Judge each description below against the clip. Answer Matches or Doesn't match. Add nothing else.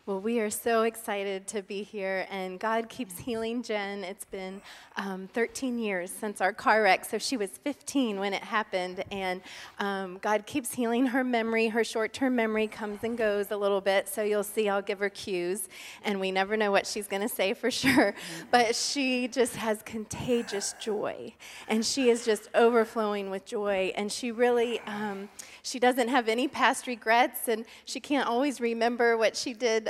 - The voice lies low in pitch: Doesn't match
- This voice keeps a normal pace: Matches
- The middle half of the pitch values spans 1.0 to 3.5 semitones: Matches